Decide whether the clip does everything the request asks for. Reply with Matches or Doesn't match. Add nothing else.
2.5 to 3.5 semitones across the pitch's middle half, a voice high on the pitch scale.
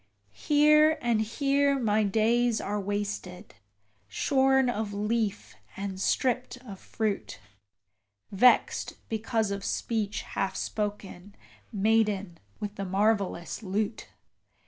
Matches